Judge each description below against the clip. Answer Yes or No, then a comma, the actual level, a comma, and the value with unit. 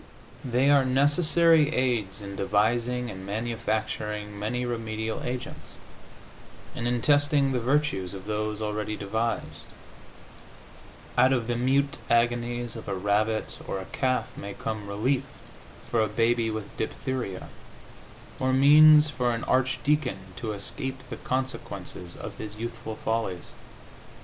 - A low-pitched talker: Yes, low, 115 Hz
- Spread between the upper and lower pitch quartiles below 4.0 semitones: Yes, average, 3.5 semitones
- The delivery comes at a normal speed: No, slow, 130 wpm